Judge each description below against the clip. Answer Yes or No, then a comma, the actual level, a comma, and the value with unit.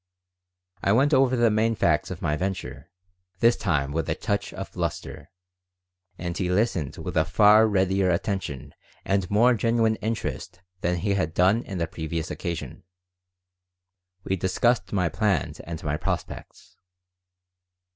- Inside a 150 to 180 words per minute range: No, average, 140 wpm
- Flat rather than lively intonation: No, average, 4.4 semitones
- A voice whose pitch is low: Yes, very low, 95 Hz